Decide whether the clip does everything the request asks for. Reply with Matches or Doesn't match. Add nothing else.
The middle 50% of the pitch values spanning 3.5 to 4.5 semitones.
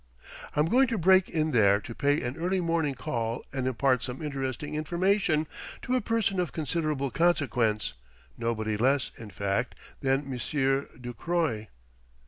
Doesn't match